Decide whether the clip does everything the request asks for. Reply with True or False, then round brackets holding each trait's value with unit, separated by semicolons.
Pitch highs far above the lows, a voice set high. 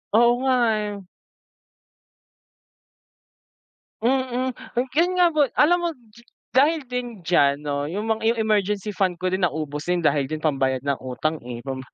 True (8.8 semitones; 205 Hz)